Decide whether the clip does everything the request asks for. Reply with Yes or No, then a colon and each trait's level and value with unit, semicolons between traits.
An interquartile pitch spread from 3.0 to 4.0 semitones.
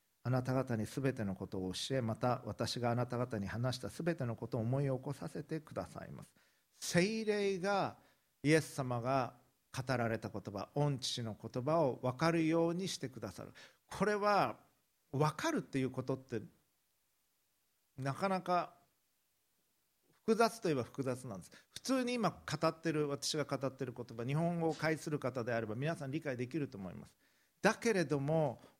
No: average, 5.1 semitones